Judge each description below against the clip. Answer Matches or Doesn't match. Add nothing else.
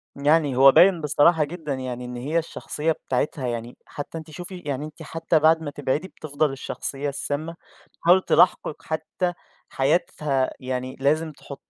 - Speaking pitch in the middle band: Matches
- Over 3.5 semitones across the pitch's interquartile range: Doesn't match